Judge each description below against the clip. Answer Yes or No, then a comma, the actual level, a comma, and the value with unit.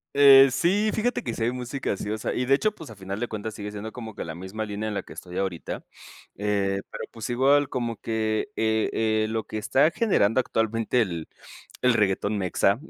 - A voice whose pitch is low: Yes, low, 110 Hz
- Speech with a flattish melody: No, average, 3.6 semitones